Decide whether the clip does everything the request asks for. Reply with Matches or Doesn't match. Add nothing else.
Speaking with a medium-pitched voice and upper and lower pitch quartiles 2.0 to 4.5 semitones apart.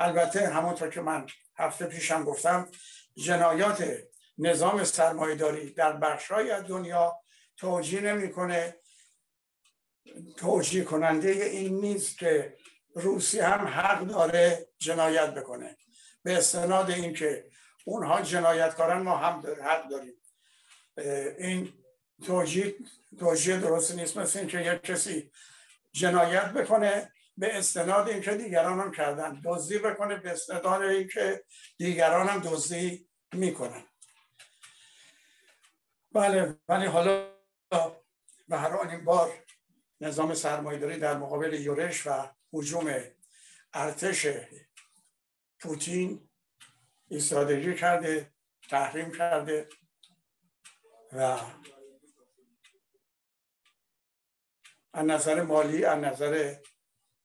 Matches